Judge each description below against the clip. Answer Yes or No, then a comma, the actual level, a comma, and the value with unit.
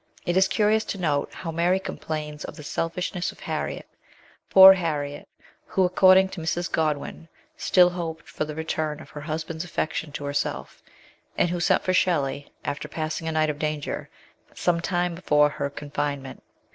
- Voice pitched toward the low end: No, medium, 160 Hz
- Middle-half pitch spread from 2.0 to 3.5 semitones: Yes, average, 3.0 semitones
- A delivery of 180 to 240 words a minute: No, average, 170 wpm